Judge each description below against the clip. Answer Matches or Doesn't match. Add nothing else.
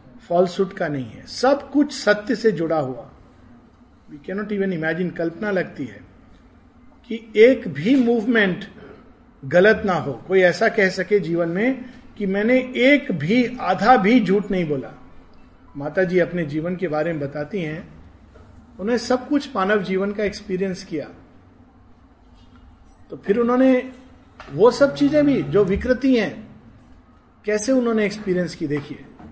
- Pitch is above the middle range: Matches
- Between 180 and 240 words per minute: Doesn't match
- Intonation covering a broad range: Matches